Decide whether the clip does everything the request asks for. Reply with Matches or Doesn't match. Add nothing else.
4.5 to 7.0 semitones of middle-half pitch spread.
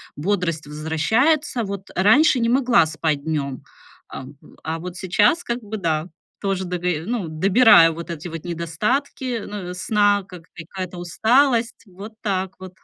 Matches